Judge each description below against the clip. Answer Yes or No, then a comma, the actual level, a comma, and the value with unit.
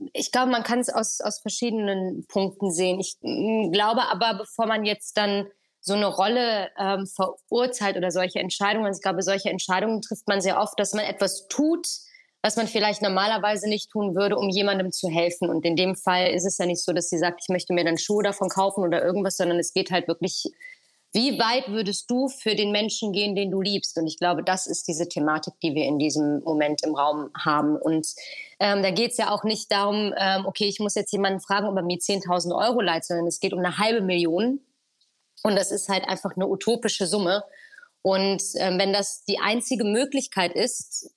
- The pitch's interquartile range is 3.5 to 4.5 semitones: No, narrow, 2.6 semitones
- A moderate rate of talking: No, fast, 210 wpm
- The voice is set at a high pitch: Yes, high, 195 Hz